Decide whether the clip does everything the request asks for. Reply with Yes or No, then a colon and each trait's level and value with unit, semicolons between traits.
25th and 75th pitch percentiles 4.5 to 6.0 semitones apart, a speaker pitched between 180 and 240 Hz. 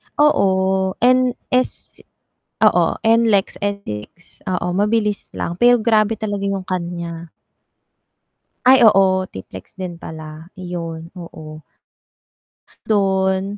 No: average, 3.7 semitones; high, 190 Hz